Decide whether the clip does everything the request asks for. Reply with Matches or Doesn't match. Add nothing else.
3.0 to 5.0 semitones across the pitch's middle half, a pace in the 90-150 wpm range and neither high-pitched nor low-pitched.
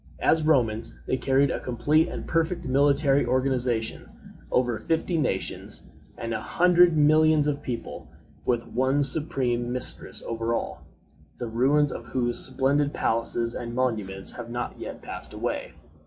Doesn't match